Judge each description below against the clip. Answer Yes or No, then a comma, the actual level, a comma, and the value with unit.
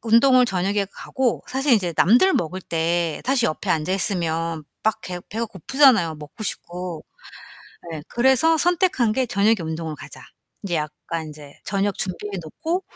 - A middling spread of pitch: No, wide, 6.8 semitones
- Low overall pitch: No, high, 195 Hz